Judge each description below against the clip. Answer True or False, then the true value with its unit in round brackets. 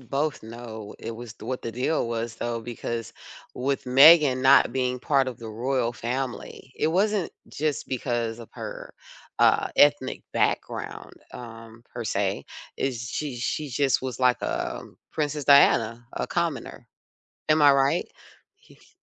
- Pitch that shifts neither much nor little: True (3.0 semitones)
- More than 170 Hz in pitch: False (125 Hz)